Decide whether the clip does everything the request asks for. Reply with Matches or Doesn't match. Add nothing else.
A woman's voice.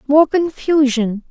Matches